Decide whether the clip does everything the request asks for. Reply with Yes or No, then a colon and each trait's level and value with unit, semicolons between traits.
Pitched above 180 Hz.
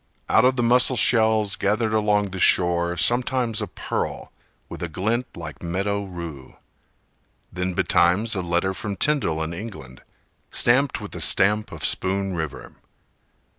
No: low, 100 Hz